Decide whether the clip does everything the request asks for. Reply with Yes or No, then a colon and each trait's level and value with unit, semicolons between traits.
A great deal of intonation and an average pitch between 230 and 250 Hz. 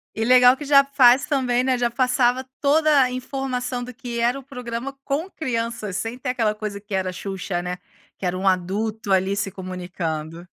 No: average, 4.9 semitones; high, 240 Hz